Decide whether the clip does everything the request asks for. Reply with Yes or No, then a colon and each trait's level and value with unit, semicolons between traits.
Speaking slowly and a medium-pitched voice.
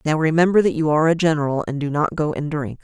No: fast, 275 wpm; medium, 155 Hz